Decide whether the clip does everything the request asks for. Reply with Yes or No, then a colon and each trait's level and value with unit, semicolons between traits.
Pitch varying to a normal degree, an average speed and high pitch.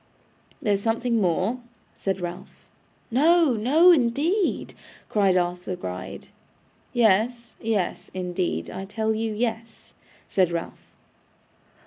No: average, 4.5 semitones; slow, 100 wpm; high, 220 Hz